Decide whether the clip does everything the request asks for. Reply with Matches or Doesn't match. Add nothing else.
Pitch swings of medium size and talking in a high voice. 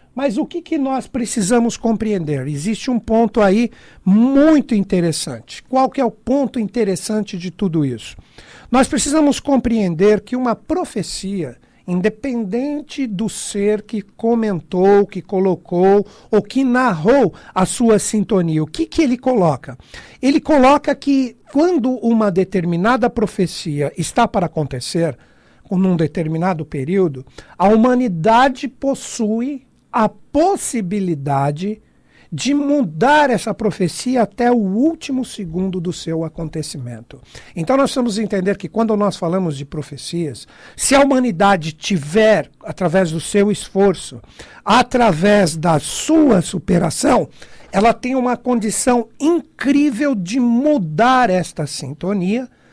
Doesn't match